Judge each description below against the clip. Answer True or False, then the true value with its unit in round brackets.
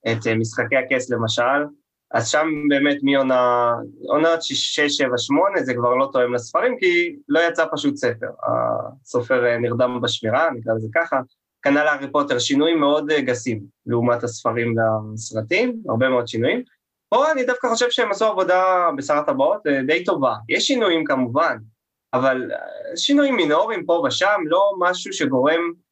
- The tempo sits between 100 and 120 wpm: False (145 wpm)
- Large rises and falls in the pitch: True (5.8 semitones)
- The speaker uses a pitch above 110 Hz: True (140 Hz)